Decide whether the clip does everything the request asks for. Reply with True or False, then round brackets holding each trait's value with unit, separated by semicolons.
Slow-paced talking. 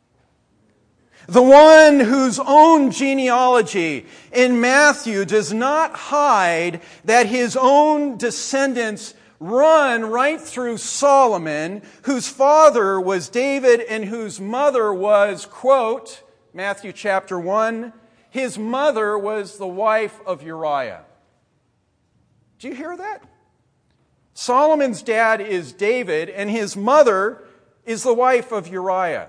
True (110 wpm)